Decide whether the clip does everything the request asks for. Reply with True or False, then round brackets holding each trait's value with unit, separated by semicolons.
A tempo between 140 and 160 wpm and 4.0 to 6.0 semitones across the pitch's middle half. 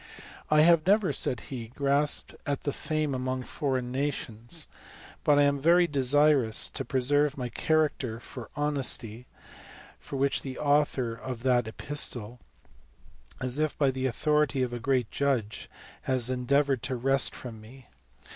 False (145 wpm; 2.8 semitones)